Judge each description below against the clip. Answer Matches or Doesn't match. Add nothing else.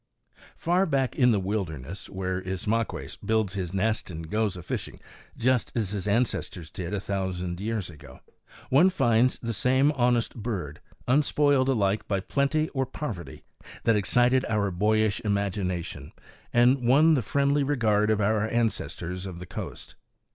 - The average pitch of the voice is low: Matches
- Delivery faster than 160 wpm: Doesn't match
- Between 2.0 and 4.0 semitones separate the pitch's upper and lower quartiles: Doesn't match